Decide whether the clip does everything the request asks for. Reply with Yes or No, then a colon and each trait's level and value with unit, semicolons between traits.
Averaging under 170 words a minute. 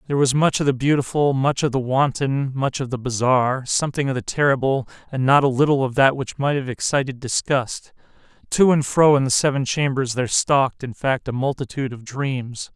No: fast, 205 wpm